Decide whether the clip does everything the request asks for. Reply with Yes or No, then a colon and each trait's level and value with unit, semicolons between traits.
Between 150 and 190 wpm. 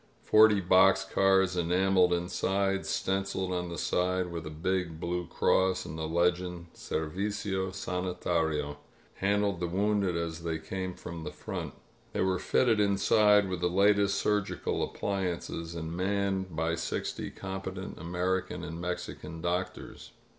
No: average, 140 wpm